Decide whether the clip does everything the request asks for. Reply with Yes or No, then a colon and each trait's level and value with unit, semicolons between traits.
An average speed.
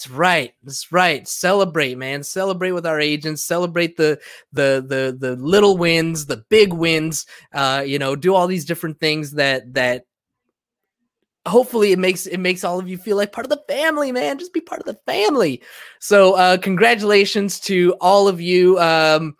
Yes: average, 185 wpm